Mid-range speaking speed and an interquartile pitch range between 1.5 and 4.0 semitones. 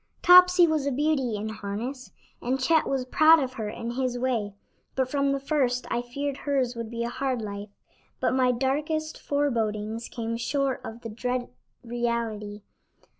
Yes: average, 170 wpm; average, 3.3 semitones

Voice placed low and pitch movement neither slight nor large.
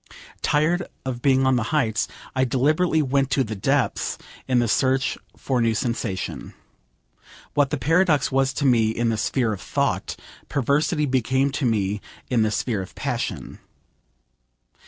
Yes: low, 130 Hz; average, 3.6 semitones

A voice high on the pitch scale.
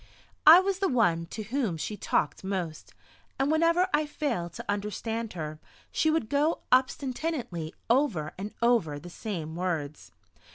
Yes: high, 220 Hz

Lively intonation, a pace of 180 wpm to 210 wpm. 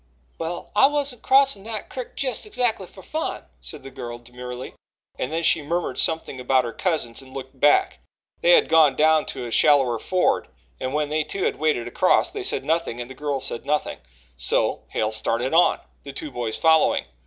Yes: wide, 5.9 semitones; average, 195 wpm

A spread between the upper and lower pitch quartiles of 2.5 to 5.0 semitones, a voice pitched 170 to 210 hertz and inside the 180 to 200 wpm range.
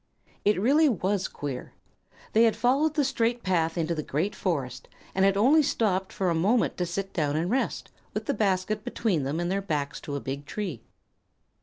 No: wide, 5.5 semitones; high, 190 Hz; average, 195 wpm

